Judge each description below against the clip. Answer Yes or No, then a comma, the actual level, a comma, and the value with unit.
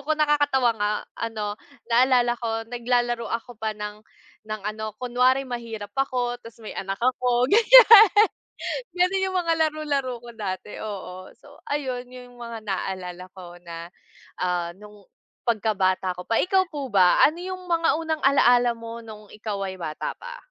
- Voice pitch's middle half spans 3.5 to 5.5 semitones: Yes, average, 4.5 semitones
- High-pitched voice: Yes, high, 235 Hz